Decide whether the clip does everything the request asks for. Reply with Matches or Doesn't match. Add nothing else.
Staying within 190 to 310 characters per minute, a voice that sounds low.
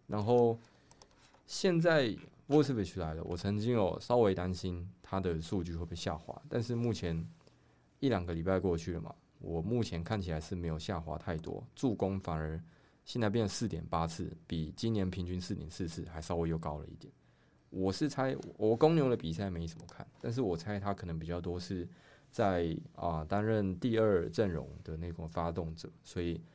Matches